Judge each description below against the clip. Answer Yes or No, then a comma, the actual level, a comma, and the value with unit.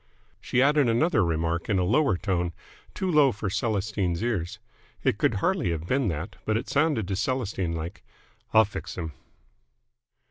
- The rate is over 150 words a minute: Yes, average, 165 wpm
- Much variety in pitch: Yes, wide, 6.4 semitones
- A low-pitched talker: Yes, low, 100 Hz